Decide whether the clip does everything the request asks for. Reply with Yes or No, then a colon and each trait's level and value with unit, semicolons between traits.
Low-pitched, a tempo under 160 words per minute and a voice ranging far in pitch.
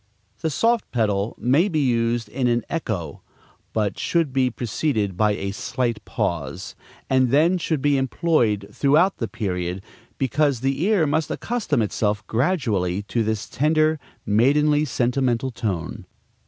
Yes: low, 125 Hz; average, 140 wpm; wide, 6.1 semitones